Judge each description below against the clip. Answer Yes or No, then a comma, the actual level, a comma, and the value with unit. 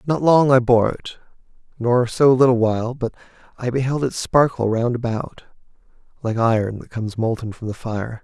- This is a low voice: Yes, low, 120 Hz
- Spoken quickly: No, average, 175 wpm